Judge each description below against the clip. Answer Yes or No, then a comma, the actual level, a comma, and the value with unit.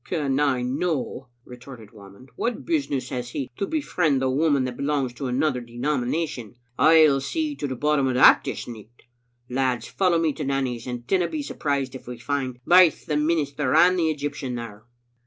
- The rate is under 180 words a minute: No, average, 185 wpm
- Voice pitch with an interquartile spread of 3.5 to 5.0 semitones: Yes, average, 3.9 semitones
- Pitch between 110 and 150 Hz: Yes, low, 135 Hz